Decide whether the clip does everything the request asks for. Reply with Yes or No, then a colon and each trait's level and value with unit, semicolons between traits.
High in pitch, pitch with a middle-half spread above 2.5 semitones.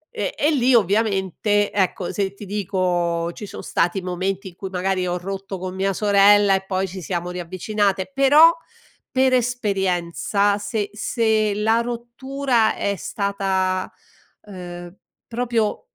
Yes: high, 200 Hz; average, 2.9 semitones